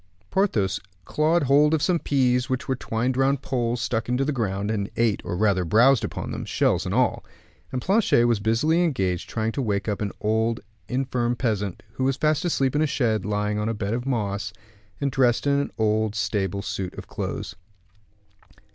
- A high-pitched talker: No, low, 120 Hz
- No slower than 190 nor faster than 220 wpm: Yes, average, 195 wpm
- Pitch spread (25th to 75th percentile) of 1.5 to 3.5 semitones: No, average, 4.4 semitones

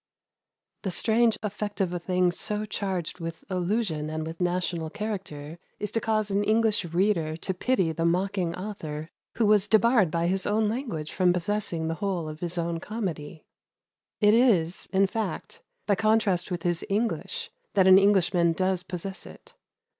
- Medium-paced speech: Yes, average, 165 wpm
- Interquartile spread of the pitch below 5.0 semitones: Yes, average, 3.7 semitones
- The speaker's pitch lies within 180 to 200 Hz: Yes, medium, 185 Hz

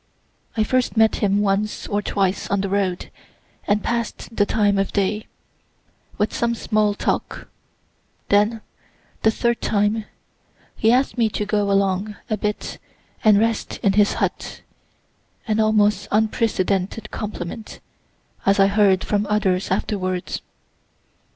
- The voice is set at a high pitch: Yes, high, 210 Hz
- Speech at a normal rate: No, slow, 130 wpm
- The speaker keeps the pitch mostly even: Yes, narrow, 1.7 semitones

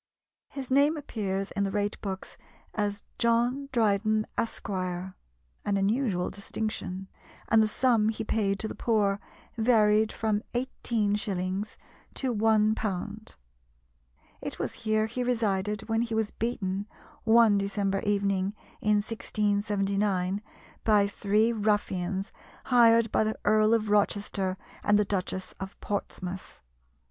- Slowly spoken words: Yes, slow, 120 wpm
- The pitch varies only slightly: Yes, narrow, 2.1 semitones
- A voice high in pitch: Yes, high, 210 Hz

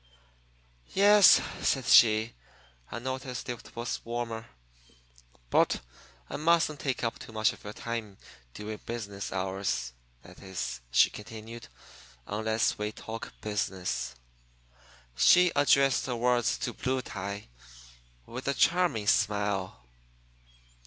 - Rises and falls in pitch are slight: No, average, 3.6 semitones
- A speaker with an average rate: No, slow, 115 wpm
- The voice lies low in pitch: Yes, low, 115 Hz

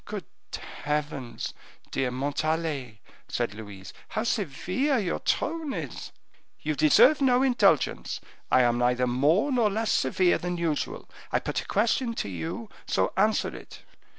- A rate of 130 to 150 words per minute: Yes, average, 140 wpm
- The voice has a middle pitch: Yes, medium, 165 Hz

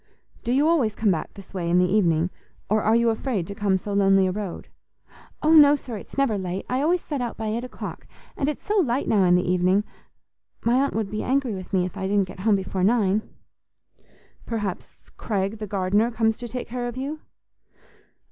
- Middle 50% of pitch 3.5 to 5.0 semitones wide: Yes, average, 4.4 semitones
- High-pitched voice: Yes, high, 215 Hz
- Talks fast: Yes, fast, 215 wpm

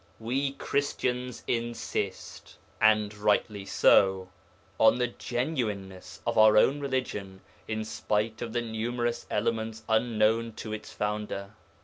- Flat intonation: Yes, narrow, 2.3 semitones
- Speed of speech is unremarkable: No, slow, 115 wpm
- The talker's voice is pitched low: Yes, low, 110 Hz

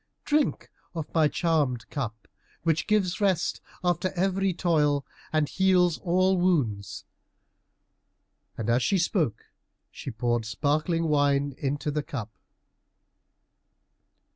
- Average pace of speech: No, slow, 110 wpm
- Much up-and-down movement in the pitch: No, average, 4.8 semitones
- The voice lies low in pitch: No, medium, 155 Hz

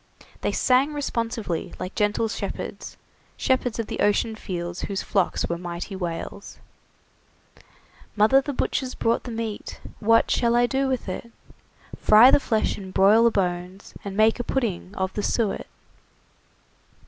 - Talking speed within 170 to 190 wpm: No, average, 150 wpm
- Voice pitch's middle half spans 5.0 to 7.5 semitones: No, average, 3.8 semitones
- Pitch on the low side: No, high, 215 Hz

